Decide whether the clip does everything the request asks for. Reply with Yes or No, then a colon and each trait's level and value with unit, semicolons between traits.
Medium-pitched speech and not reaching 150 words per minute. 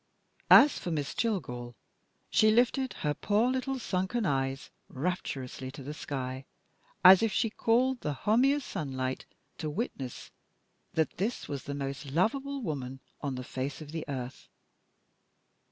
Yes: medium, 155 Hz; average, 140 wpm